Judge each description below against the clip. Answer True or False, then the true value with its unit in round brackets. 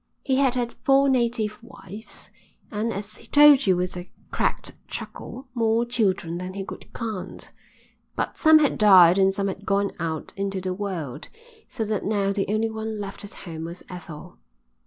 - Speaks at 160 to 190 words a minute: True (180 wpm)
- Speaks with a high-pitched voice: True (205 Hz)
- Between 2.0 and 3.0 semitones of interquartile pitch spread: False (3.8 semitones)